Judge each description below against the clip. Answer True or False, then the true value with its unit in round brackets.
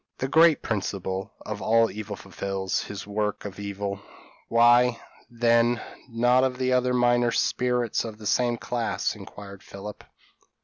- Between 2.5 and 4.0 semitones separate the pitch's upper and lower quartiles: True (3.2 semitones)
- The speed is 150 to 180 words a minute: False (140 wpm)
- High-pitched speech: False (115 Hz)